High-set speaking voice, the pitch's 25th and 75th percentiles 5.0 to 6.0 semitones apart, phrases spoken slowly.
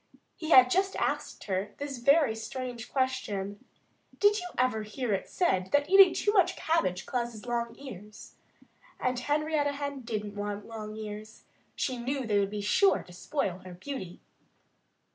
No: high, 240 Hz; wide, 5.5 semitones; average, 155 wpm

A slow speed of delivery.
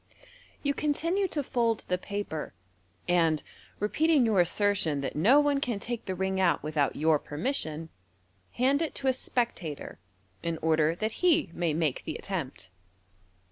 No: average, 155 wpm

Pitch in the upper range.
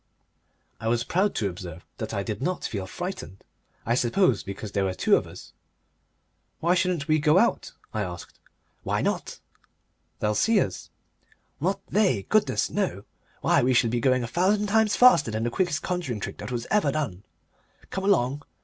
No: low, 130 Hz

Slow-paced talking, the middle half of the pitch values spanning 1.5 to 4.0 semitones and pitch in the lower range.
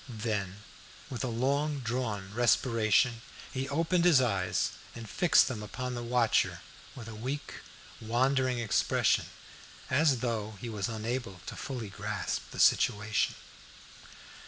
Yes: slow, 130 wpm; average, 3.2 semitones; low, 120 Hz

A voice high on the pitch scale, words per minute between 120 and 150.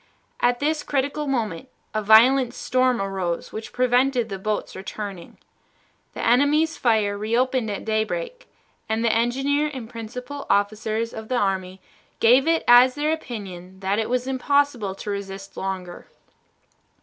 Yes: high, 230 Hz; average, 140 wpm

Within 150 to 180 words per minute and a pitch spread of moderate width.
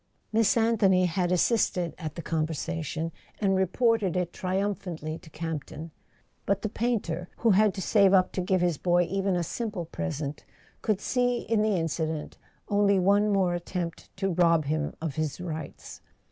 Yes: average, 170 wpm; average, 3.6 semitones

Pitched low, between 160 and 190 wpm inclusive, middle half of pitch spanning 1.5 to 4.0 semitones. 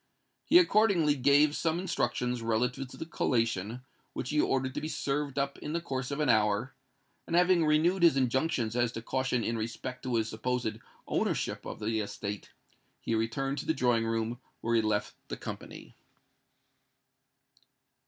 No: low, 125 Hz; average, 170 wpm; average, 4.7 semitones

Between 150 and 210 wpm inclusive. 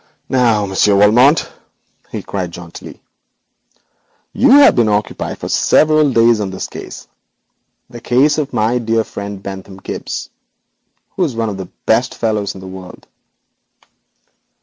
No: average, 140 wpm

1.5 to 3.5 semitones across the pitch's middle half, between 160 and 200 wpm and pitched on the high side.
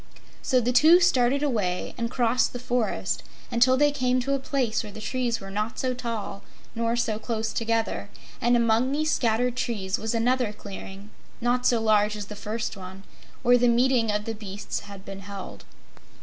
Yes: average, 3.0 semitones; average, 185 wpm; high, 230 Hz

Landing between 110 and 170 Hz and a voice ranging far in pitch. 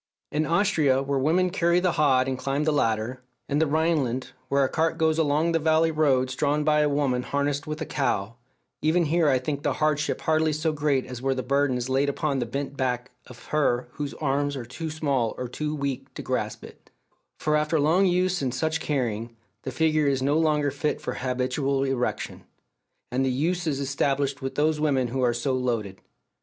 No: medium, 140 Hz; average, 3.0 semitones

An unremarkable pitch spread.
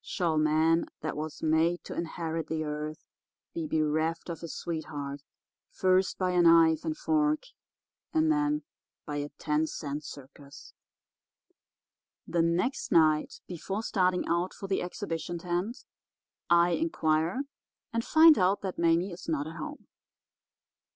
Yes: average, 3.0 semitones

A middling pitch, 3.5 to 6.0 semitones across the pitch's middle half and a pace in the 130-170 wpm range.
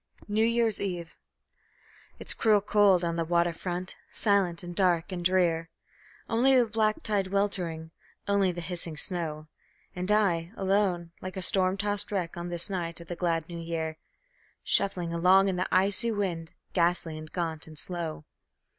No: medium, 180 Hz; average, 3.0 semitones; average, 165 wpm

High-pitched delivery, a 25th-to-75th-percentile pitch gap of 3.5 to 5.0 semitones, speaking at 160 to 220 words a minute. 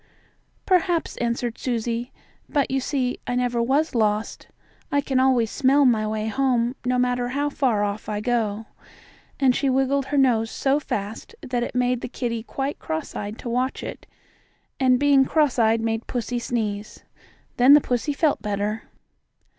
No: high, 245 Hz; average, 3.1 semitones; average, 165 wpm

